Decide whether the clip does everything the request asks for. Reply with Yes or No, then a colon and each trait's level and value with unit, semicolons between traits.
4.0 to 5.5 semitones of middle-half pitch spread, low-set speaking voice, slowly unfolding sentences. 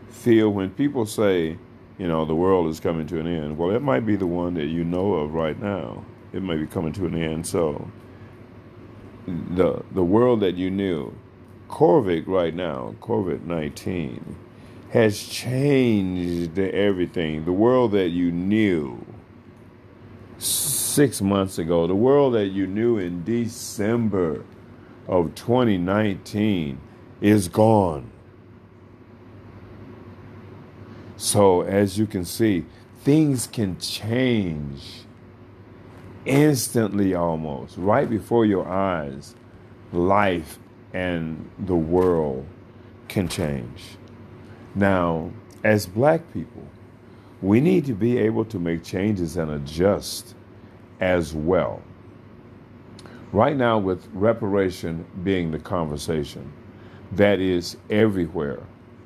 Yes: average, 4.7 semitones; low, 100 Hz; slow, 115 wpm